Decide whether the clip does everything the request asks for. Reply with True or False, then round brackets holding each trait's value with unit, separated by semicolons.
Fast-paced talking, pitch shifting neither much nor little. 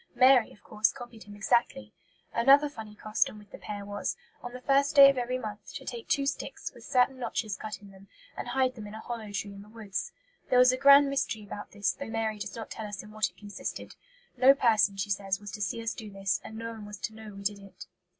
True (250 wpm; 3.4 semitones)